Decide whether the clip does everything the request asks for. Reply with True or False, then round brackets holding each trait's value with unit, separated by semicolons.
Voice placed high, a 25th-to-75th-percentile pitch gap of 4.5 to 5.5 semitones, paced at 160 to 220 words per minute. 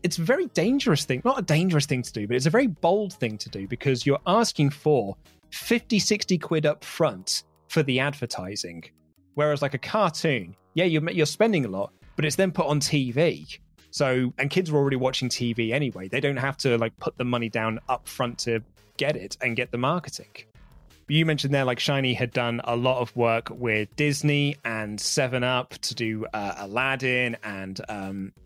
False (130 Hz; 5.0 semitones; 200 wpm)